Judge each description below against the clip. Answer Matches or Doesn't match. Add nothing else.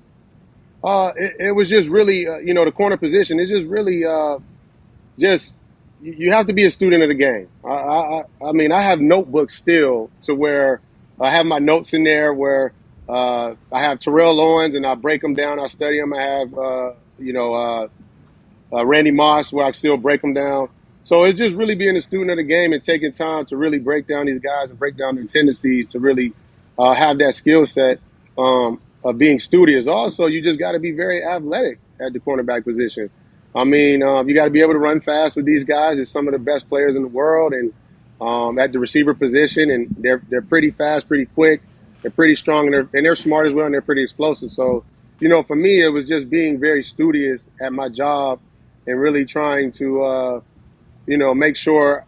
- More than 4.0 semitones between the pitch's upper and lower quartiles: Doesn't match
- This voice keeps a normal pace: Doesn't match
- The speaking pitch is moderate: Matches